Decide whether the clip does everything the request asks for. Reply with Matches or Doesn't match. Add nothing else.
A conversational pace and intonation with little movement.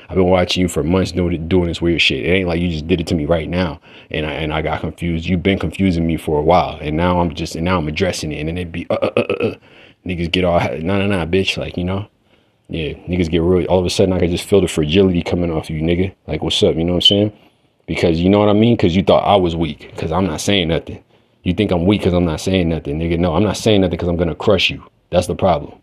Doesn't match